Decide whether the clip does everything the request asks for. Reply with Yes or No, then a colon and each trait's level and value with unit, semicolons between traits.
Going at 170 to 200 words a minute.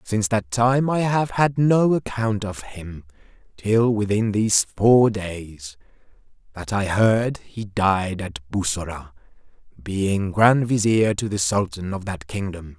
No: average, 145 wpm